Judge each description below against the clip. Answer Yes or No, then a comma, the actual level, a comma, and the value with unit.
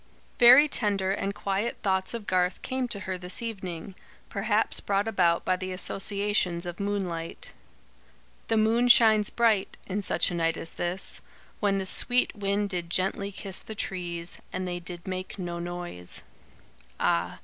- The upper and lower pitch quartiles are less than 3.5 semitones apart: Yes, average, 2.8 semitones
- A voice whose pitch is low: No, high, 190 Hz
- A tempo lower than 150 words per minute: No, average, 160 wpm